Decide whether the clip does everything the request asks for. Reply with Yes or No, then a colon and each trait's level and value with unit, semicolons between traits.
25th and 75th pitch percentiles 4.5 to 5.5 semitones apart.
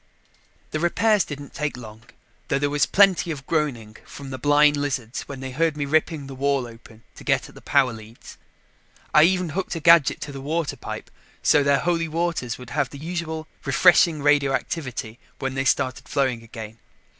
No: average, 3.7 semitones